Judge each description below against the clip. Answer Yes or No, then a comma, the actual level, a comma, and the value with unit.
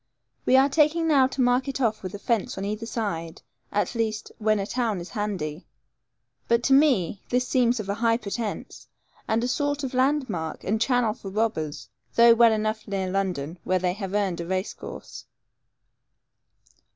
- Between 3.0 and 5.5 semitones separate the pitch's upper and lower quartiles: Yes, average, 4.2 semitones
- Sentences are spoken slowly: No, average, 180 wpm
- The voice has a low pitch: No, high, 220 Hz